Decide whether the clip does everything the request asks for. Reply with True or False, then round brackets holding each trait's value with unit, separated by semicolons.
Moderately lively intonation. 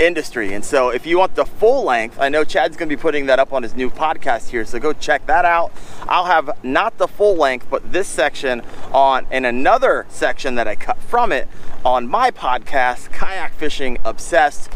True (4.1 semitones)